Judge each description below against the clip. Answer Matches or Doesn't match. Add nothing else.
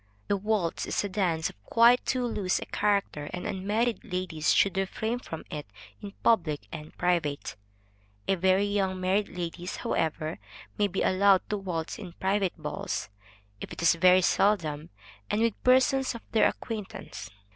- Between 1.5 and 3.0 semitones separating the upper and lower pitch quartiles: Doesn't match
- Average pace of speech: Matches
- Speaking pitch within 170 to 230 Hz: Matches